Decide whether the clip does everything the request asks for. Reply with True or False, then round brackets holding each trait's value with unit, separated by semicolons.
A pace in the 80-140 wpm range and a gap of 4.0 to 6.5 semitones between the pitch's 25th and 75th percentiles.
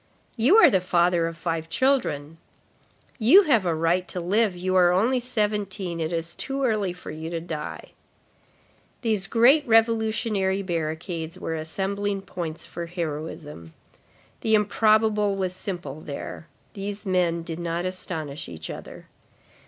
True (135 wpm; 4.5 semitones)